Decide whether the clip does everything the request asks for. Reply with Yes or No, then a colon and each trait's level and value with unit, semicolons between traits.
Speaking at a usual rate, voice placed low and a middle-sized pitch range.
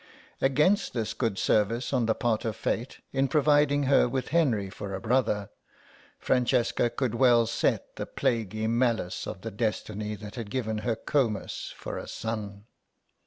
Yes: average, 160 wpm; low, 115 Hz; average, 3.4 semitones